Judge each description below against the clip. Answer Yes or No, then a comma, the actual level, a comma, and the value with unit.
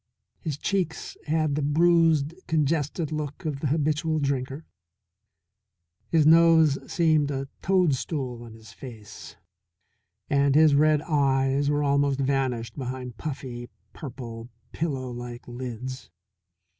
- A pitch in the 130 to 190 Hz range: Yes, medium, 140 Hz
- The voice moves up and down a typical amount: Yes, average, 3.2 semitones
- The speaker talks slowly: Yes, slow, 115 wpm